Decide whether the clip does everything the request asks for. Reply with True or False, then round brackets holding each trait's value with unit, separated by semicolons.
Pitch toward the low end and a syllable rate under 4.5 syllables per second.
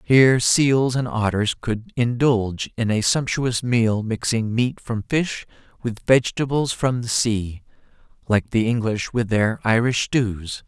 True (115 Hz; 4.0 syllables/s)